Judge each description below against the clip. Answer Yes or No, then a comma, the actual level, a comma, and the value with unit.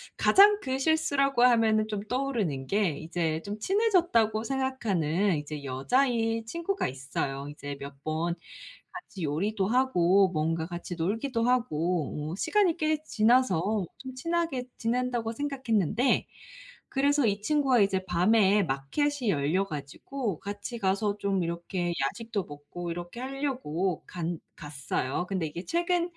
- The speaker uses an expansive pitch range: Yes, wide, 7.5 semitones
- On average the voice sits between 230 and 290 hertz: No, high, 205 Hz